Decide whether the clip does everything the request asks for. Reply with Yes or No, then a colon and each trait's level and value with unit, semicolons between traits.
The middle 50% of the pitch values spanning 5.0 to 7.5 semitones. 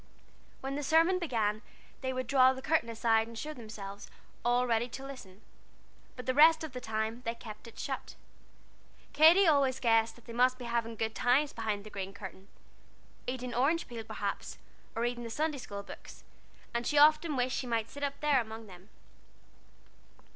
No: average, 3.7 semitones